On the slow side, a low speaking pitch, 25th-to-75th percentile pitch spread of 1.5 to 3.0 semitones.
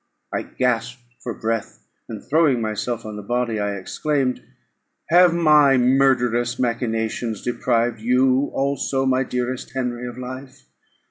Yes: slow, 130 wpm; low, 125 Hz; narrow, 2.4 semitones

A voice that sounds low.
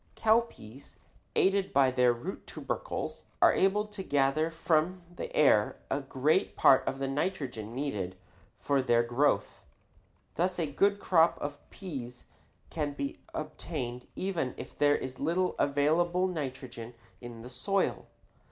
No: medium, 145 Hz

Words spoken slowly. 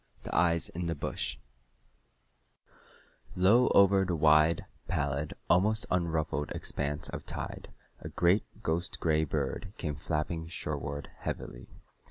Yes: slow, 120 wpm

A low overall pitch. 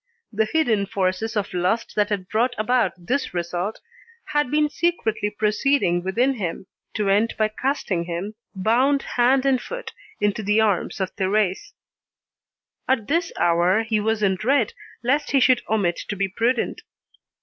No: high, 215 Hz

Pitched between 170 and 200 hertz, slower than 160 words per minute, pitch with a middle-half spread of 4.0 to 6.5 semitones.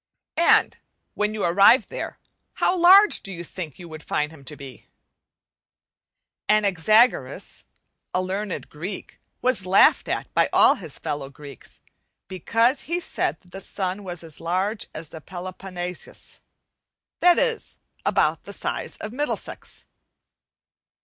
Yes: medium, 185 Hz; slow, 135 wpm; average, 4.5 semitones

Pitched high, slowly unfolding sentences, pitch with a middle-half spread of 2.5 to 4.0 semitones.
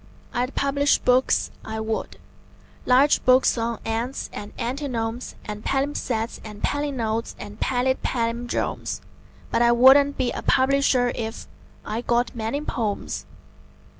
Yes: high, 245 Hz; slow, 125 wpm; average, 2.9 semitones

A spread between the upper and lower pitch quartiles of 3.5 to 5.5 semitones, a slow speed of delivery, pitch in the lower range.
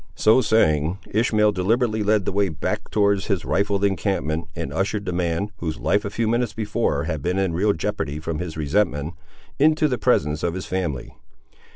No: average, 4.7 semitones; average, 185 wpm; very low, 95 Hz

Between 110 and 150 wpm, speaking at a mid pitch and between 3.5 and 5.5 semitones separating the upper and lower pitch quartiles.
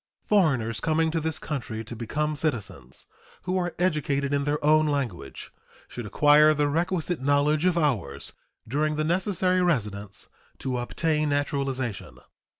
Yes: average, 140 wpm; medium, 150 Hz; average, 4.4 semitones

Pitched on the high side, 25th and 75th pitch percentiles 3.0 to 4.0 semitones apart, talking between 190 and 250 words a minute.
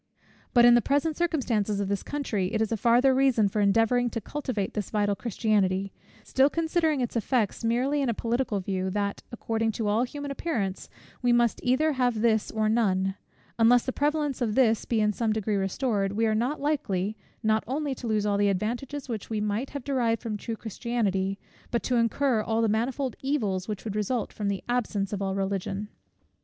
Yes: high, 225 Hz; average, 3.7 semitones; average, 195 wpm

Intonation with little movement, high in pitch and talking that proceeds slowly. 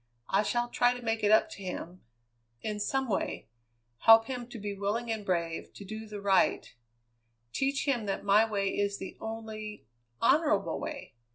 No: narrow, 2.3 semitones; high, 215 Hz; average, 175 wpm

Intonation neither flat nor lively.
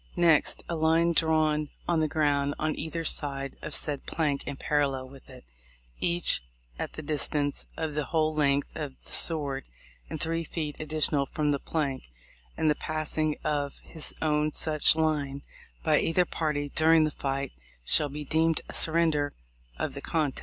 No: narrow, 1.8 semitones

